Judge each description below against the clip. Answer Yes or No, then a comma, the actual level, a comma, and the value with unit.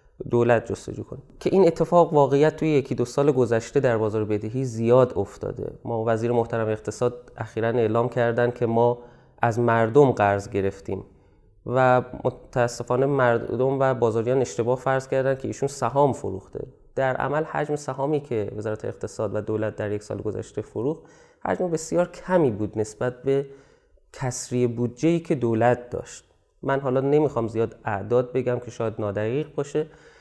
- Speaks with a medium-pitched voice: No, low, 120 Hz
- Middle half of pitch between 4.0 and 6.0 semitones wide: No, average, 3.1 semitones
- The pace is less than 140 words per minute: No, fast, 155 wpm